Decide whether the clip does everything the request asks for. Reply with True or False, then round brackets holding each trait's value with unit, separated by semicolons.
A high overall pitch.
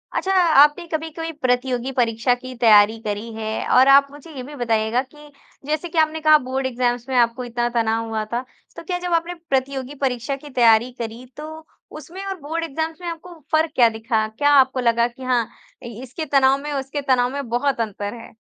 True (260 Hz)